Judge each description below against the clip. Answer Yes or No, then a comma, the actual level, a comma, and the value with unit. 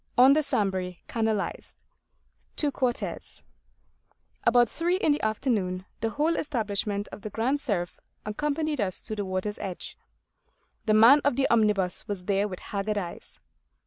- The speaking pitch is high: Yes, high, 215 Hz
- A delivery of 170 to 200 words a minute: No, average, 145 wpm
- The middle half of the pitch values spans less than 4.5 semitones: No, average, 5.2 semitones